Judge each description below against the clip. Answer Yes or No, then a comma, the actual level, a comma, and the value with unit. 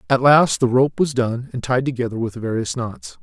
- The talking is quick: Yes, fast, 225 wpm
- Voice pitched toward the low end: Yes, low, 125 Hz